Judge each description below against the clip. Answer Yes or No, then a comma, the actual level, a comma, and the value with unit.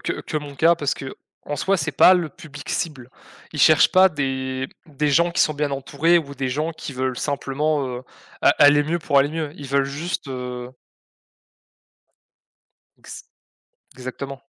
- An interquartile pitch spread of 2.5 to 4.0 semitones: Yes, average, 2.8 semitones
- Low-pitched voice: No, medium, 145 Hz